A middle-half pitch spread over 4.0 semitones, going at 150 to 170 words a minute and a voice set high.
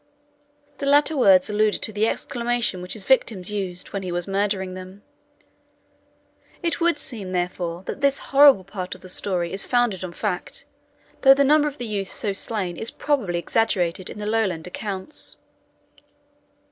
Yes: average, 4.7 semitones; average, 165 wpm; high, 205 Hz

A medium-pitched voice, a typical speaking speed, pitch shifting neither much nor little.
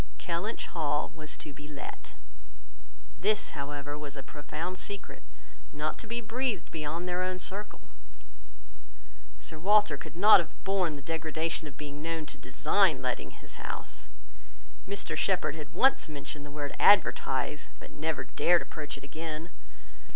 Yes: medium, 160 Hz; average, 150 wpm; average, 3.9 semitones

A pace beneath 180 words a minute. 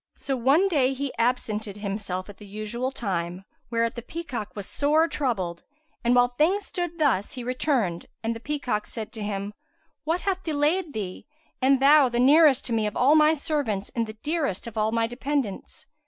No: average, 185 wpm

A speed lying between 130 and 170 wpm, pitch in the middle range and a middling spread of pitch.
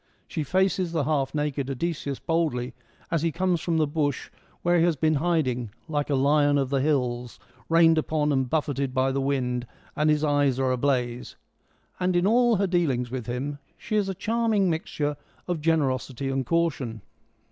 No: average, 180 wpm; medium, 145 Hz; average, 3.9 semitones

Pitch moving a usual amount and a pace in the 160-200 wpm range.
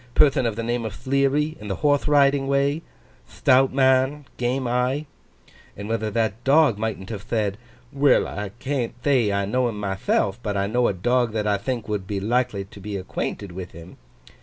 Yes: average, 4.7 semitones; average, 185 wpm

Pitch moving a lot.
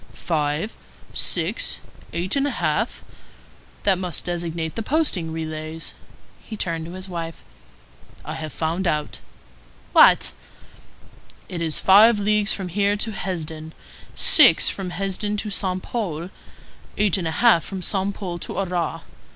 No: average, 3.8 semitones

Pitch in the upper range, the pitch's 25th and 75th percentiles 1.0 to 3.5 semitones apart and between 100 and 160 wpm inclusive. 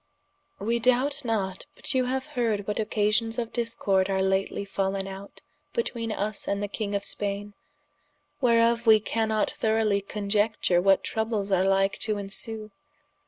Yes: high, 210 Hz; narrow, 2.6 semitones; average, 155 wpm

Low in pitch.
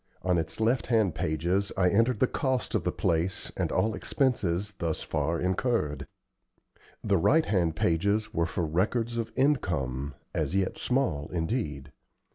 Yes: very low, 95 Hz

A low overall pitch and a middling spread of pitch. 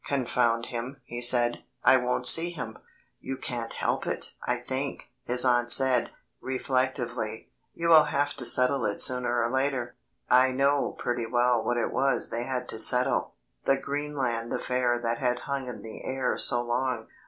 No: low, 125 Hz; narrow, 1.7 semitones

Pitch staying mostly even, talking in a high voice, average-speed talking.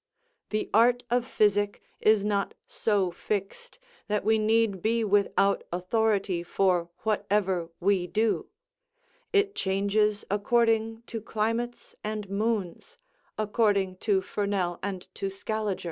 No: narrow, 2.2 semitones; high, 210 Hz; slow, 115 wpm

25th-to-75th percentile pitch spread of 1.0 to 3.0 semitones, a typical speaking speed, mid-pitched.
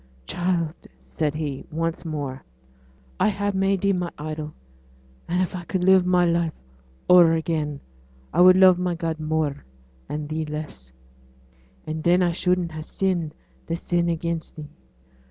Yes: narrow, 2.6 semitones; average, 155 wpm; medium, 165 Hz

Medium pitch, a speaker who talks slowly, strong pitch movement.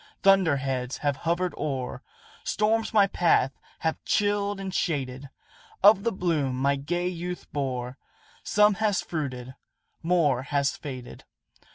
Yes: medium, 160 Hz; slow, 130 wpm; wide, 6.2 semitones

